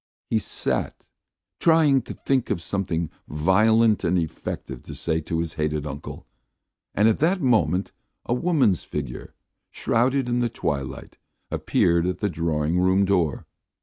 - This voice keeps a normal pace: Yes, average, 145 wpm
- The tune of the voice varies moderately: No, wide, 6.6 semitones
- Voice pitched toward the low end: Yes, very low, 95 Hz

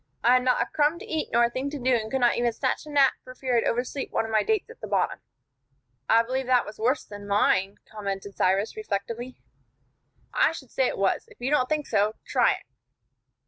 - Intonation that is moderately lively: Yes, average, 3.7 semitones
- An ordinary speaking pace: No, fast, 230 wpm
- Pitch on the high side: Yes, high, 245 Hz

